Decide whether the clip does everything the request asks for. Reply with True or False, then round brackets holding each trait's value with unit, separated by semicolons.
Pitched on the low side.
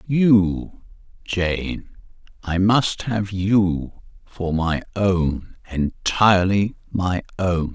True (95 Hz)